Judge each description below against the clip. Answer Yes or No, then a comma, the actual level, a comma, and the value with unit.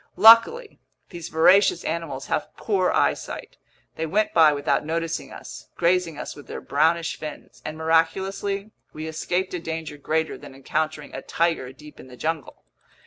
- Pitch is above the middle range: No, medium, 160 Hz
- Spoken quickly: No, average, 155 wpm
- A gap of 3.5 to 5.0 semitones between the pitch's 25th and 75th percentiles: No, average, 2.9 semitones